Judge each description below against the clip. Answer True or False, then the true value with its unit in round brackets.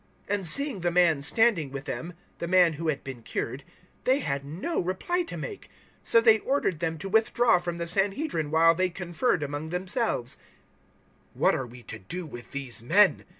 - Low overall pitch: False (175 Hz)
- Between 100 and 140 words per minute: False (195 wpm)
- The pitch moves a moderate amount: False (5.8 semitones)